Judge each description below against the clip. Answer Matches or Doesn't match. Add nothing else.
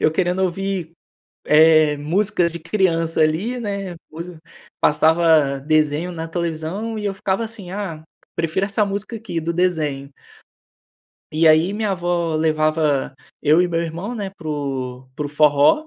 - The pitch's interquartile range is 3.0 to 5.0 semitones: Matches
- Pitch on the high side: Doesn't match